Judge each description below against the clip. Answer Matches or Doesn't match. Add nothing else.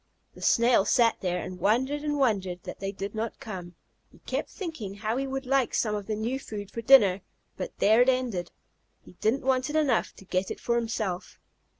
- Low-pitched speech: Doesn't match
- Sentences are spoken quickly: Matches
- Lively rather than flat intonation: Doesn't match